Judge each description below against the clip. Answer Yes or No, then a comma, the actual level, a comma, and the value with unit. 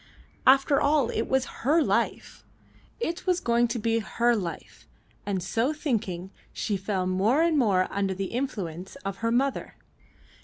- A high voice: Yes, high, 230 Hz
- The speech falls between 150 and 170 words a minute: Yes, average, 155 wpm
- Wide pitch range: Yes, wide, 5.9 semitones